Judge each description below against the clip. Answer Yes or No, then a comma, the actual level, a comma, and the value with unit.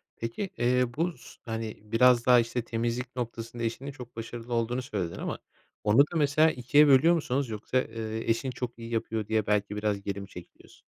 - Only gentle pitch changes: Yes, narrow, 2.3 semitones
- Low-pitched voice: Yes, low, 115 Hz